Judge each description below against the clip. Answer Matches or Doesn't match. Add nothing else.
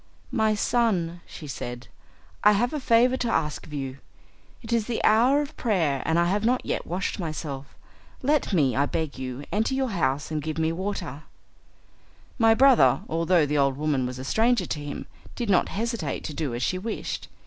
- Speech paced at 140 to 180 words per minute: Doesn't match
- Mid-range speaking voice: Matches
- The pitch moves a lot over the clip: Matches